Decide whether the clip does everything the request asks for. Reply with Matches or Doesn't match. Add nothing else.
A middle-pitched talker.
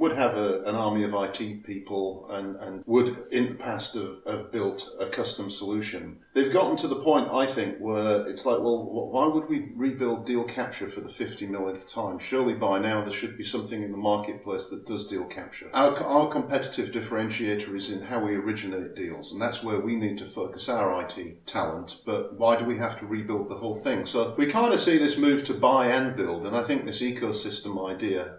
Doesn't match